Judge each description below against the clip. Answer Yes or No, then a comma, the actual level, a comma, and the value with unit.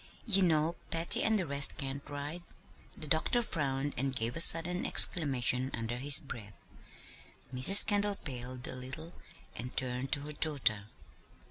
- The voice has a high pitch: No, medium, 140 Hz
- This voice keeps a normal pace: Yes, average, 150 wpm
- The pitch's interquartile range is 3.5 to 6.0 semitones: Yes, average, 4.4 semitones